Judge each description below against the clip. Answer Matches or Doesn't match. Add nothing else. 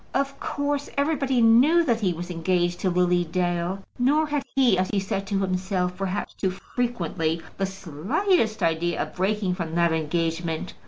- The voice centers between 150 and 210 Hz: Matches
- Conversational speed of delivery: Matches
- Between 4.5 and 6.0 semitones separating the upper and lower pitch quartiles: Matches